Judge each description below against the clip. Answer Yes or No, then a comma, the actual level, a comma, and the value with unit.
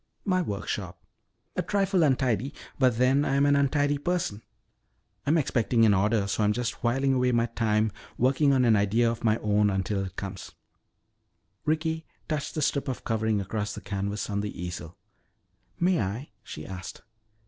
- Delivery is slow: No, average, 170 wpm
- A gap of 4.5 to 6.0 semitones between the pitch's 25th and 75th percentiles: Yes, wide, 5.4 semitones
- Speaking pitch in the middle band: No, low, 115 Hz